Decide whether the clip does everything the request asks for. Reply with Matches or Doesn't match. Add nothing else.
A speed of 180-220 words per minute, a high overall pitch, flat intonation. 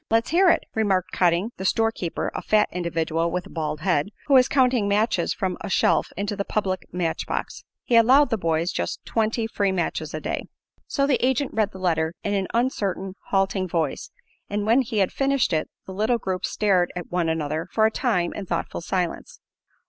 Doesn't match